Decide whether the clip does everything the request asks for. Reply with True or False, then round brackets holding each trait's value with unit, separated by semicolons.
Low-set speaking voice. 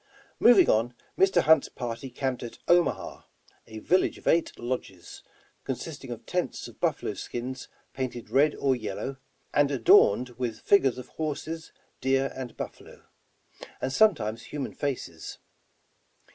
True (130 Hz)